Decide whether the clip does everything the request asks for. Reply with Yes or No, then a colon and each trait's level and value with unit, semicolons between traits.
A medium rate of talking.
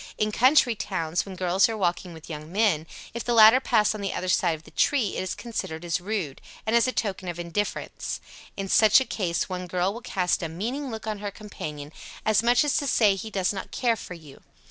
No: fast, 235 wpm